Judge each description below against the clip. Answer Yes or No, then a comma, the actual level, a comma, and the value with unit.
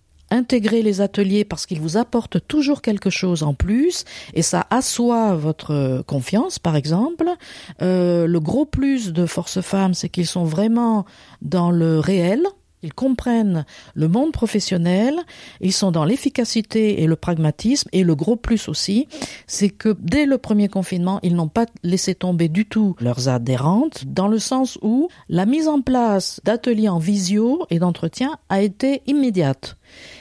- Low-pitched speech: No, high, 200 Hz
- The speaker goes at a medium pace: Yes, average, 160 wpm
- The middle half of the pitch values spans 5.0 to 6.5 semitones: Yes, wide, 5.5 semitones